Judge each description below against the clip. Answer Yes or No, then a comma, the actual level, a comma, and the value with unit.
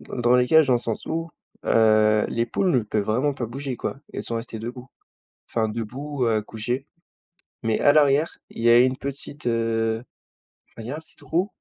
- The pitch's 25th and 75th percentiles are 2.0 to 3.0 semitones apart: No, average, 3.6 semitones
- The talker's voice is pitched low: Yes, low, 120 Hz